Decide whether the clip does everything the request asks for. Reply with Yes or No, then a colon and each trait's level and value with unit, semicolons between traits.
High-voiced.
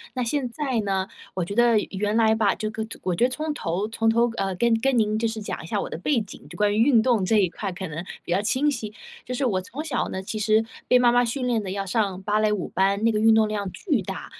Yes: high, 220 Hz